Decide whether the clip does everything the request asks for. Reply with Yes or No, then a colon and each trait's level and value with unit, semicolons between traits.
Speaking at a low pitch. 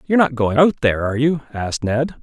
Yes: low, 130 Hz